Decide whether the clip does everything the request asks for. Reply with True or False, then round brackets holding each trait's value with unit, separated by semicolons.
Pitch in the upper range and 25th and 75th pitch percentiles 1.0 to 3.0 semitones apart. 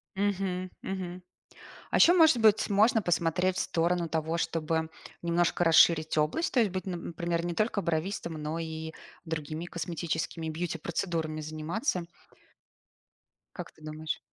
False (170 Hz; 2.7 semitones)